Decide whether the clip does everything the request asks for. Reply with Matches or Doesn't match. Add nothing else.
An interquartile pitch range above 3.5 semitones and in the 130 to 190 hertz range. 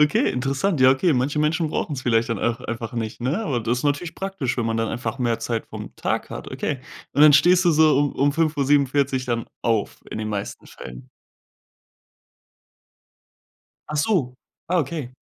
Matches